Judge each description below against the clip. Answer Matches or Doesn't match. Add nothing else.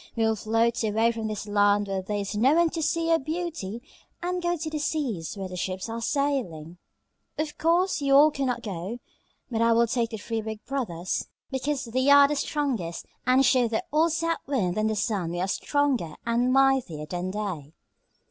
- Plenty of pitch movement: Matches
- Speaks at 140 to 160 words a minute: Doesn't match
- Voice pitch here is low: Doesn't match